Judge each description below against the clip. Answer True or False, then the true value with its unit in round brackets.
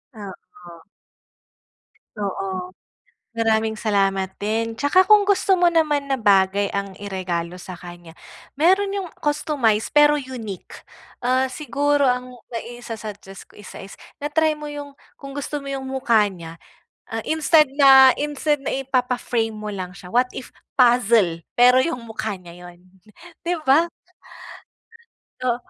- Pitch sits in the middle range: False (240 Hz)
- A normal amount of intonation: False (6.4 semitones)